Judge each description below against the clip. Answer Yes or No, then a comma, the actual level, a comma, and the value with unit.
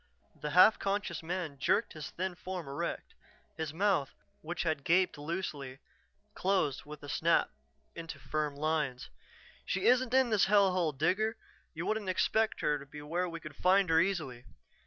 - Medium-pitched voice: Yes, medium, 170 Hz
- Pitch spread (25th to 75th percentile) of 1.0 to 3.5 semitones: No, average, 4.2 semitones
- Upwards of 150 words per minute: Yes, average, 165 wpm